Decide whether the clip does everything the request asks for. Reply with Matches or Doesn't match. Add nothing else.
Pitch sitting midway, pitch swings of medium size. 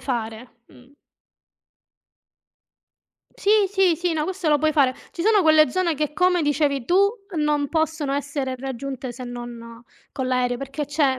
Doesn't match